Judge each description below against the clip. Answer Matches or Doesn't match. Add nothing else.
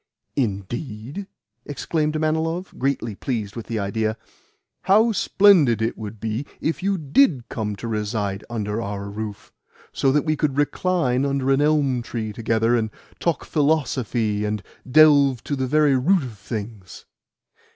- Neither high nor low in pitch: Doesn't match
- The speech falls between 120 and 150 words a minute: Matches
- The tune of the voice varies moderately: Doesn't match